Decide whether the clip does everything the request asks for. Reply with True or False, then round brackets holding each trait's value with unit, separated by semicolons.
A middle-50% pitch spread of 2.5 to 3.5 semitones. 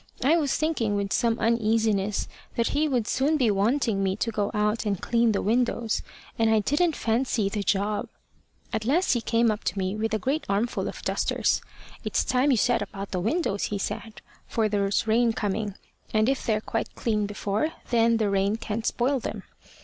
True (2.8 semitones)